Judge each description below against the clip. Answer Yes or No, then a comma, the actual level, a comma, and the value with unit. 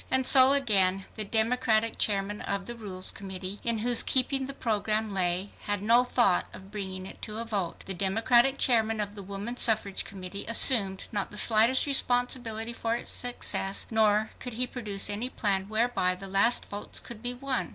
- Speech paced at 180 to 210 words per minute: Yes, average, 185 wpm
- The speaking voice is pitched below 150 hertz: No, high, 215 Hz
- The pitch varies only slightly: No, average, 3.4 semitones